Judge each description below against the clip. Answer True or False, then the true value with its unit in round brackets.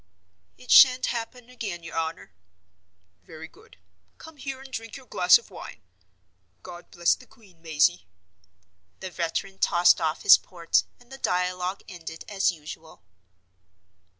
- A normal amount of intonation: False (6.4 semitones)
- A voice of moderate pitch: True (180 Hz)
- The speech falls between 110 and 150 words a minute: True (140 wpm)